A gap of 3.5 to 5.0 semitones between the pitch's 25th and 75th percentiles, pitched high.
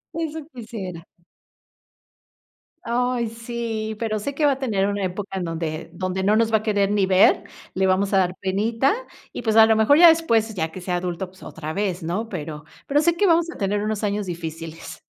Yes: average, 3.8 semitones; high, 205 Hz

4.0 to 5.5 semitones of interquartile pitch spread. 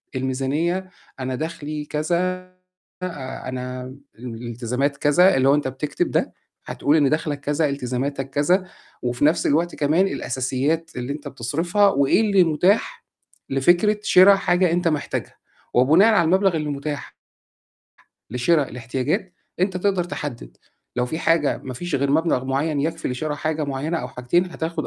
Yes: average, 4.5 semitones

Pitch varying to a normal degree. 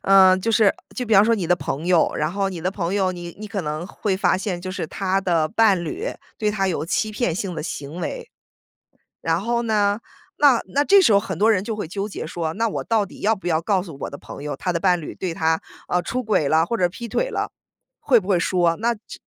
Yes: average, 3.8 semitones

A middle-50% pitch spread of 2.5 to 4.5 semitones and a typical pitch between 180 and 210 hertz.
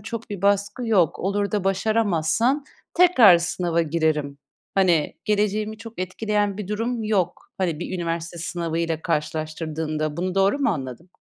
Yes: average, 4.2 semitones; medium, 185 Hz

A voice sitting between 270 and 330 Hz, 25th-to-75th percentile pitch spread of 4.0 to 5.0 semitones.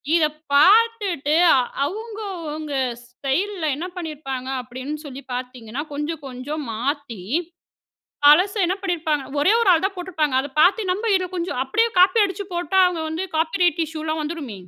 Yes: very high, 315 Hz; average, 4.5 semitones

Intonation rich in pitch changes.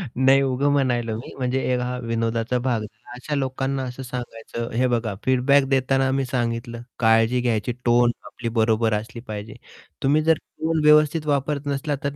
No: average, 2.8 semitones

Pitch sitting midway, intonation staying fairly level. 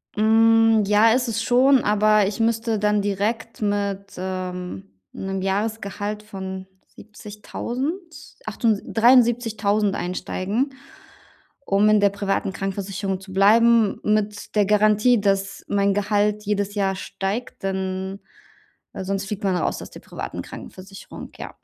No: high, 205 Hz; narrow, 2.3 semitones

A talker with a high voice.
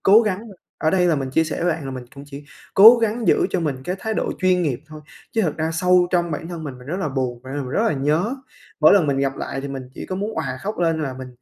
No: medium, 160 Hz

